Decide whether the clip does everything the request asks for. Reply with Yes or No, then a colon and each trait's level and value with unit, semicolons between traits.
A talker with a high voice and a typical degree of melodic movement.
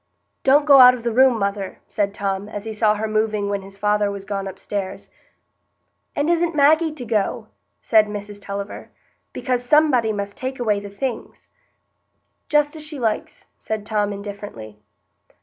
Yes: high, 215 Hz; average, 4.2 semitones